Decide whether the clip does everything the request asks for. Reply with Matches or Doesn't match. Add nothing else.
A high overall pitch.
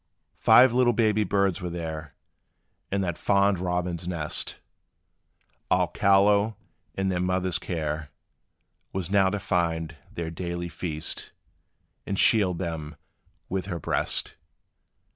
Doesn't match